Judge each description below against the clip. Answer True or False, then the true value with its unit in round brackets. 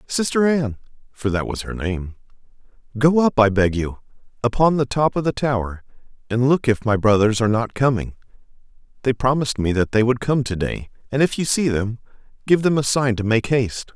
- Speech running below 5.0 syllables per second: False (5.4 syllables/s)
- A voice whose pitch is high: False (120 Hz)